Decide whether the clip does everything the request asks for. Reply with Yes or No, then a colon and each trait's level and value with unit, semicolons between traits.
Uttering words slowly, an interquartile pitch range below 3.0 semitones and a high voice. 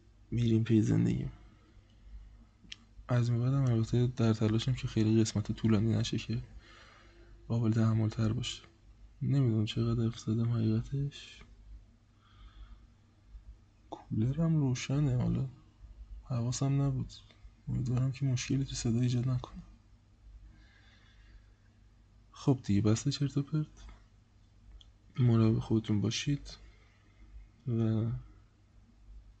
No: slow, 90 wpm; narrow, 2.5 semitones; low, 110 Hz